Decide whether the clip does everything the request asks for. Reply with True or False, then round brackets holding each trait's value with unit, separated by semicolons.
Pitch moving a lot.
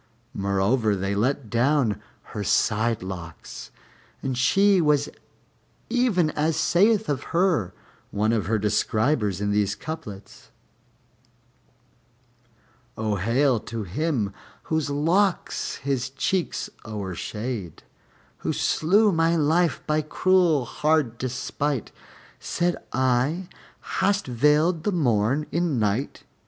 True (7.1 semitones)